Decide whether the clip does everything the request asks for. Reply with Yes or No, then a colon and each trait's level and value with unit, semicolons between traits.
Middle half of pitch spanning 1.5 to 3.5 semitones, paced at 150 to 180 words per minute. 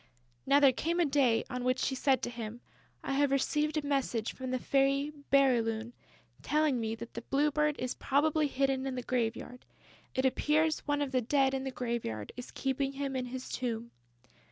No: narrow, 2.6 semitones; average, 200 wpm